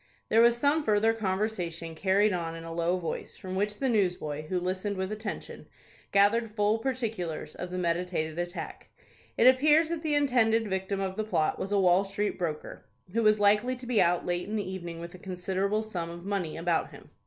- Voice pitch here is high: Yes, high, 195 Hz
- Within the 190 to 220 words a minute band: Yes, average, 200 wpm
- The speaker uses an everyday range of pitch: Yes, average, 3.9 semitones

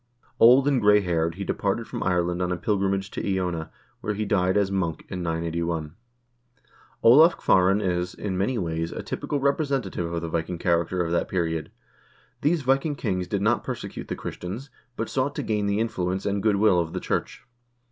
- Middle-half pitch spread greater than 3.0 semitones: Yes, average, 4.1 semitones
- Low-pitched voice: Yes, very low, 95 Hz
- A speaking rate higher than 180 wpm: Yes, average, 190 wpm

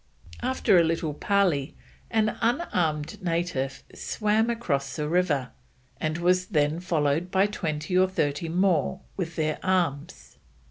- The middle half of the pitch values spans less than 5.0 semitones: Yes, average, 4.0 semitones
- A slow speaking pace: Yes, slow, 130 wpm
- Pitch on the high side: No, medium, 170 Hz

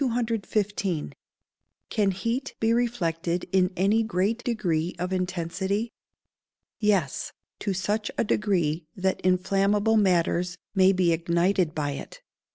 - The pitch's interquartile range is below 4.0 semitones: Yes, average, 3.2 semitones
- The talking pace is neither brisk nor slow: No, slow, 110 wpm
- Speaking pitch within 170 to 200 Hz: Yes, high, 190 Hz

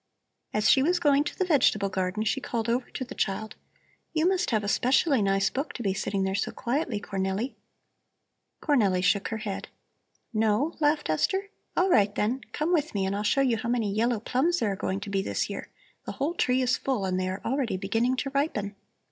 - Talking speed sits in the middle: No, fast, 215 wpm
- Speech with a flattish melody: No, wide, 5.6 semitones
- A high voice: Yes, high, 230 Hz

